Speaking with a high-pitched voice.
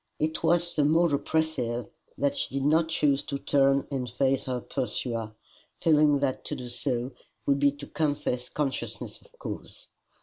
No: medium, 140 Hz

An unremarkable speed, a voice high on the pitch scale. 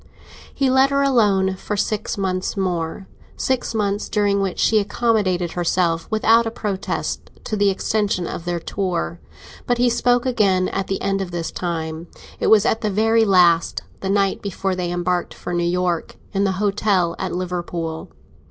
Yes: average, 170 wpm; high, 195 Hz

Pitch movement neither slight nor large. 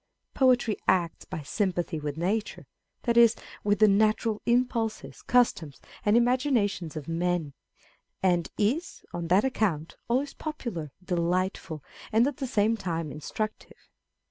No: wide, 5.7 semitones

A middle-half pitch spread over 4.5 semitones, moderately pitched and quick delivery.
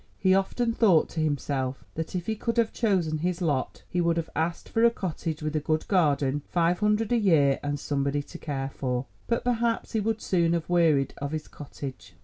Yes: average, 5.3 semitones; medium, 165 Hz; fast, 210 wpm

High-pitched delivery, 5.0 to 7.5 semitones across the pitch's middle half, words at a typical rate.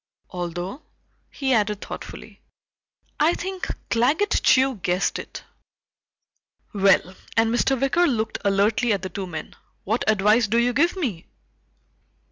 No: high, 225 Hz; wide, 5.4 semitones; slow, 125 wpm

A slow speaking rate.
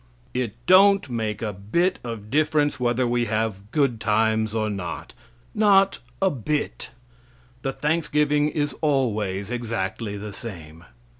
Yes: slow, 130 wpm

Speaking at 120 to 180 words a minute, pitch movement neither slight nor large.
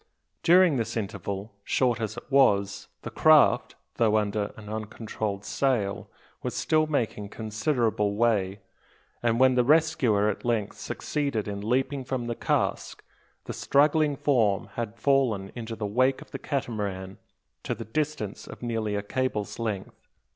Yes: average, 145 wpm; average, 4.1 semitones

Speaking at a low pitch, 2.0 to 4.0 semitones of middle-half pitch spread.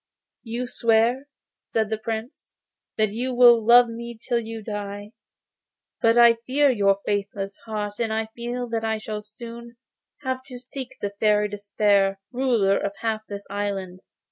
No: high, 225 Hz; narrow, 2.6 semitones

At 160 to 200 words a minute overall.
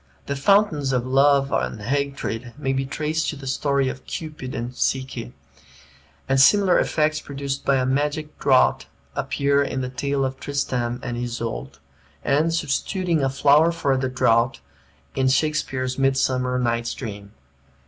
No: average, 150 wpm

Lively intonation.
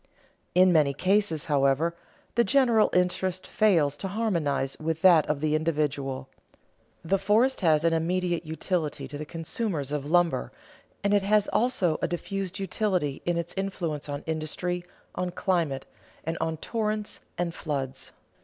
No: average, 4.2 semitones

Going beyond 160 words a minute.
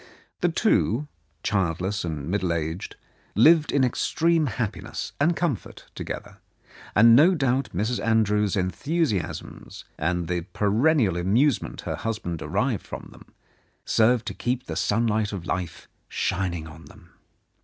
No: slow, 135 wpm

